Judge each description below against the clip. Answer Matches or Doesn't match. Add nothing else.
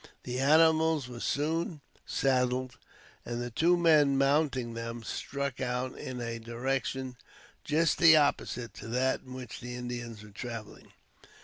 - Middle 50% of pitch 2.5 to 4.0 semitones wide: Matches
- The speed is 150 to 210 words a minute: Doesn't match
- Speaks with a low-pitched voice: Matches